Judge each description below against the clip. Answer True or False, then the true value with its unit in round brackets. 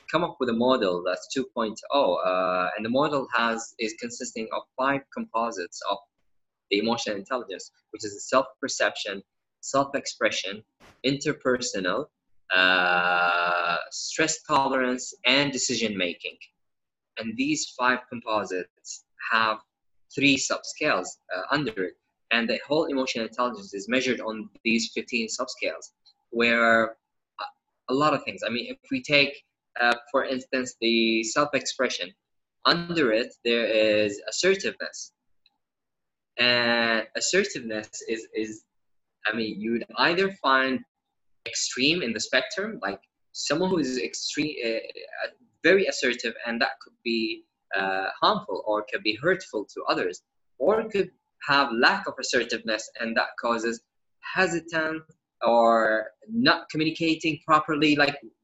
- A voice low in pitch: True (125 Hz)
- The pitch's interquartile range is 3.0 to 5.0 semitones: False (5.4 semitones)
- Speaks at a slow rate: True (125 wpm)